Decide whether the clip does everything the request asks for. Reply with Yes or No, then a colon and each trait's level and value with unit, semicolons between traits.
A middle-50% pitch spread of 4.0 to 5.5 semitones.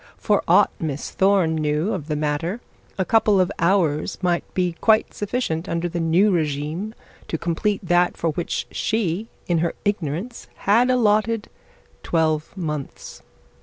Yes: average, 4.3 semitones